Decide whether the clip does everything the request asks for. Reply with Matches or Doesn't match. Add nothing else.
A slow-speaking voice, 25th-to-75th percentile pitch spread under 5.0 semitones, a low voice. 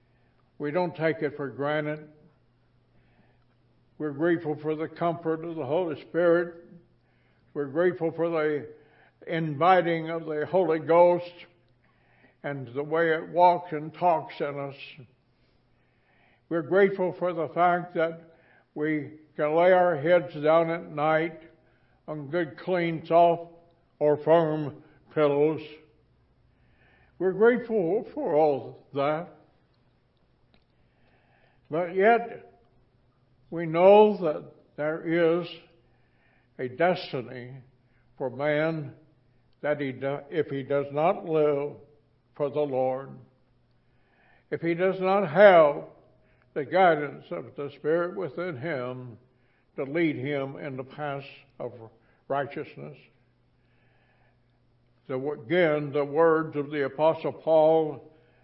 Doesn't match